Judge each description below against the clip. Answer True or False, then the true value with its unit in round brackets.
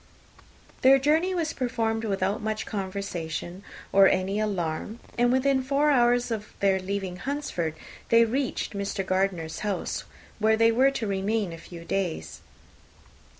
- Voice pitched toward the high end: True (210 Hz)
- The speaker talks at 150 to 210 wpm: False (140 wpm)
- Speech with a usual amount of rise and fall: True (4.3 semitones)